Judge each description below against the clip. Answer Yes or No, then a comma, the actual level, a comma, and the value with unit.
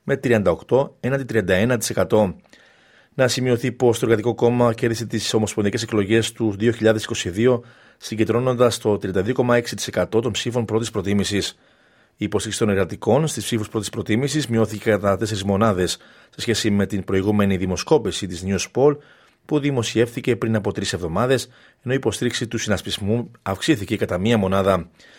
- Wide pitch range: No, average, 3.0 semitones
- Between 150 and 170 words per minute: No, average, 140 wpm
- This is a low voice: Yes, low, 110 Hz